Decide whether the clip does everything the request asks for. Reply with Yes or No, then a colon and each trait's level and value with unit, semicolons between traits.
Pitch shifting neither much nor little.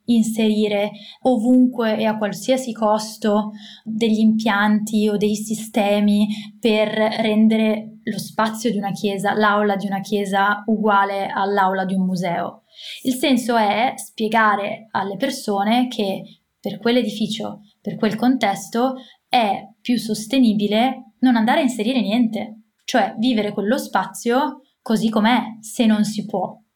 No: narrow, 2.2 semitones